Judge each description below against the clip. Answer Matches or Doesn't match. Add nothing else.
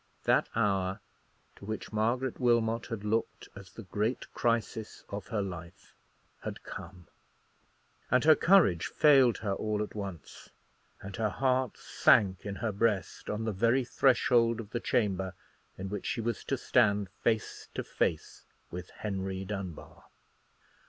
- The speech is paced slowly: Doesn't match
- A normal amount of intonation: Matches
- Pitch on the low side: Matches